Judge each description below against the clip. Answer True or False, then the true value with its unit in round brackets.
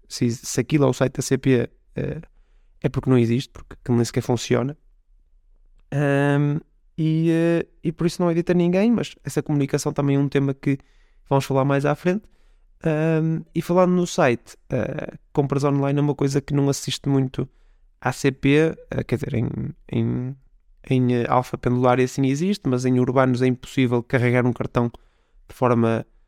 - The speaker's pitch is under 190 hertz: True (135 Hz)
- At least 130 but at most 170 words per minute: False (185 wpm)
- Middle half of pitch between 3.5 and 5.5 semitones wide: False (3.0 semitones)